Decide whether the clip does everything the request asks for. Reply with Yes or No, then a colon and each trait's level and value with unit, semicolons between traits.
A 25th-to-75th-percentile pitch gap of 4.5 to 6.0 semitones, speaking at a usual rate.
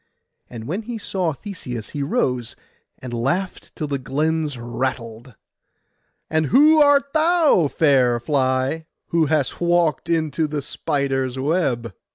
No: average, 5.1 semitones; slow, 130 wpm